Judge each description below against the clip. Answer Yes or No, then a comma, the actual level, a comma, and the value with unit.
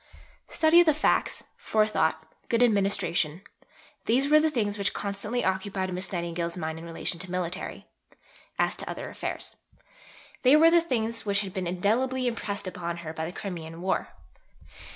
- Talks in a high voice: Yes, high, 200 Hz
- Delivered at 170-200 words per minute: No, average, 160 wpm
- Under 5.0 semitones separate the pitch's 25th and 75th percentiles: No, wide, 5.4 semitones